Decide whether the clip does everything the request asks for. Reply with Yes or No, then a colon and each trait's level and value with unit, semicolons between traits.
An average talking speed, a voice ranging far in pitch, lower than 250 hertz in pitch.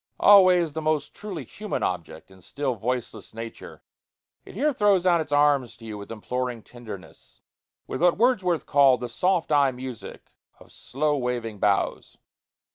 Yes: average, 155 wpm; wide, 7.0 semitones; low, 135 Hz